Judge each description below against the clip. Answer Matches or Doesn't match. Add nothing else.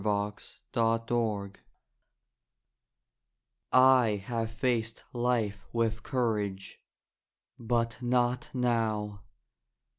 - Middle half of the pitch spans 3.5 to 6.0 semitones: Doesn't match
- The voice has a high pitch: Doesn't match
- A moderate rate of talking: Doesn't match